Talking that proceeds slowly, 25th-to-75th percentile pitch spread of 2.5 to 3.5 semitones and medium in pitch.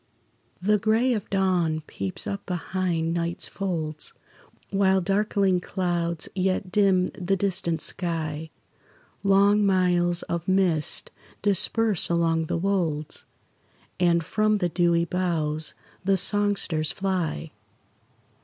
Yes: slow, 105 wpm; average, 2.8 semitones; medium, 180 Hz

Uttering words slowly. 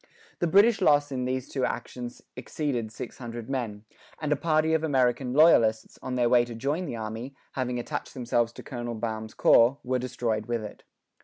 No: average, 185 wpm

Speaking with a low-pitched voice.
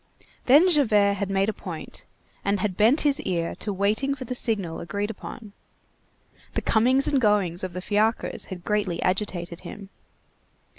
No: high, 205 Hz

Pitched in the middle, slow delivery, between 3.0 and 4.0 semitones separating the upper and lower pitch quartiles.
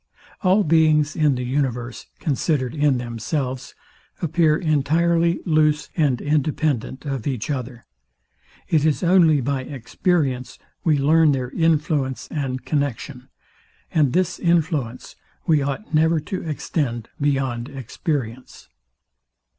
Yes: medium, 145 Hz; slow, 115 wpm; average, 3.5 semitones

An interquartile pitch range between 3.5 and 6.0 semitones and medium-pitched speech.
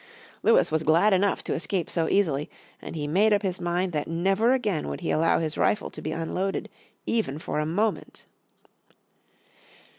Yes: average, 4.3 semitones; medium, 175 Hz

